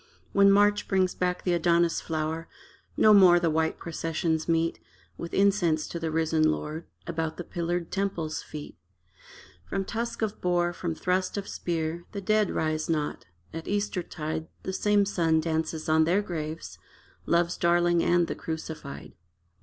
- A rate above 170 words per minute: No, average, 155 wpm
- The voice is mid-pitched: Yes, medium, 170 Hz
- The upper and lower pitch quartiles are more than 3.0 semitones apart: No, average, 2.7 semitones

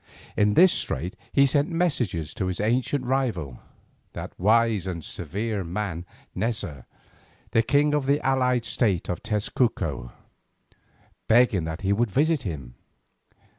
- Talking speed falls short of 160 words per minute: Yes, slow, 135 wpm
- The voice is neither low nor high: No, low, 110 Hz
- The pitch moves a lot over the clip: Yes, wide, 6.2 semitones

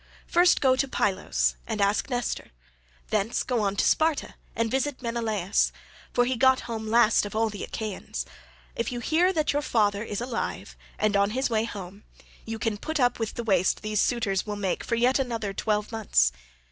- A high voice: Yes, high, 225 Hz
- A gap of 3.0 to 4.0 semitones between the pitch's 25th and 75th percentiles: Yes, average, 3.3 semitones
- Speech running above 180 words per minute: Yes, average, 190 wpm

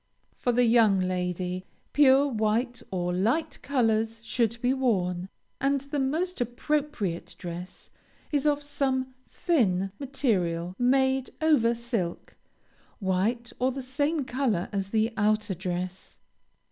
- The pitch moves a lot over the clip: Yes, wide, 5.9 semitones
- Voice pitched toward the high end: Yes, high, 235 Hz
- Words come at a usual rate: No, slow, 120 wpm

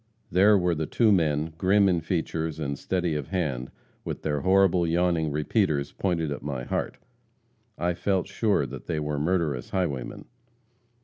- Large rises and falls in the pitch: No, average, 4.0 semitones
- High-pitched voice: No, very low, 80 Hz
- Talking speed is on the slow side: No, average, 150 wpm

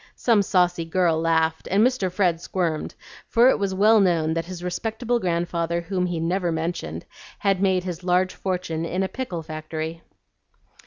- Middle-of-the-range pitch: Yes, medium, 180 Hz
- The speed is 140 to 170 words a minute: Yes, average, 165 wpm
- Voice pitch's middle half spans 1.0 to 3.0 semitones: Yes, narrow, 2.5 semitones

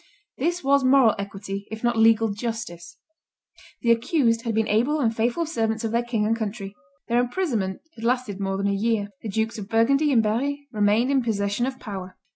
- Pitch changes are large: No, average, 3.2 semitones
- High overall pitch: Yes, high, 225 Hz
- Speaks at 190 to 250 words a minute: Yes, average, 195 wpm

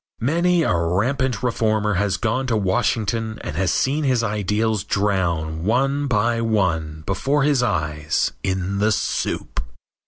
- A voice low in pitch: Yes, low, 105 Hz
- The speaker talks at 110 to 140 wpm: Yes, slow, 135 wpm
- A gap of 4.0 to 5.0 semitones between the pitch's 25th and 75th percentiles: Yes, average, 4.7 semitones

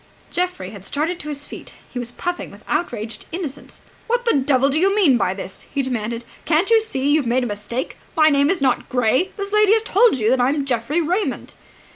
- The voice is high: Yes, very high, 280 Hz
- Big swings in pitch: Yes, wide, 6.7 semitones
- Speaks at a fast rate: Yes, fast, 220 wpm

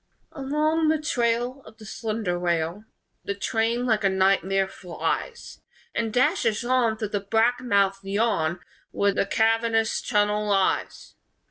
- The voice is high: Yes, high, 220 Hz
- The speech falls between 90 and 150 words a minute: Yes, slow, 135 wpm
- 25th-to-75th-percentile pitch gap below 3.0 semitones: No, average, 3.5 semitones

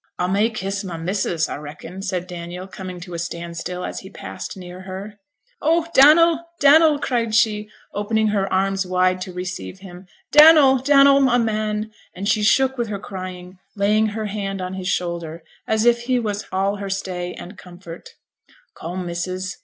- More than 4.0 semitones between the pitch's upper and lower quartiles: No, average, 3.3 semitones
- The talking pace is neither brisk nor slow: Yes, average, 175 wpm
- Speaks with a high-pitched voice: Yes, high, 195 Hz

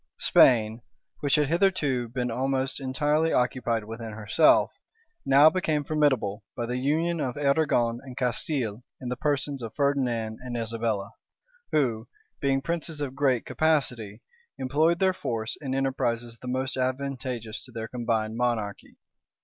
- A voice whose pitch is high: No, low, 130 Hz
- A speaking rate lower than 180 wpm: Yes, average, 140 wpm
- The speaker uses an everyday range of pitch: Yes, average, 3.7 semitones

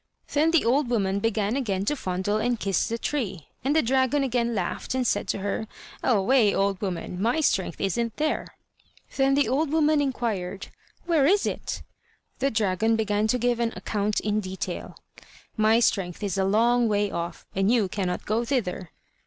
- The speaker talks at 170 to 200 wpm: Yes, average, 180 wpm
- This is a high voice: Yes, high, 225 Hz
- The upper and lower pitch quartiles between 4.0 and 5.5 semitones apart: Yes, average, 4.8 semitones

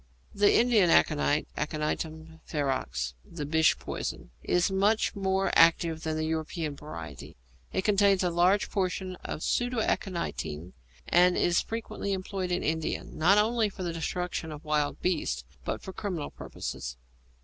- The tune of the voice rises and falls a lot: No, average, 4.0 semitones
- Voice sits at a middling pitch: Yes, medium, 170 Hz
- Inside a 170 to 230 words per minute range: No, average, 140 wpm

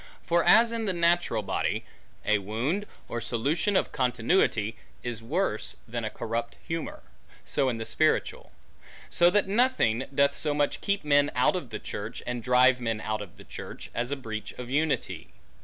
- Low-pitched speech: Yes, low, 130 Hz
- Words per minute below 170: No, average, 175 wpm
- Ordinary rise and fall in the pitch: No, wide, 7.0 semitones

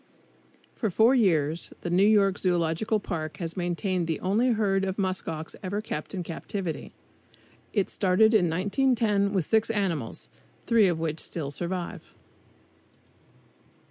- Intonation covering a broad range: No, average, 3.8 semitones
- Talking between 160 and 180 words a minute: No, average, 140 wpm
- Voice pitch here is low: No, medium, 185 Hz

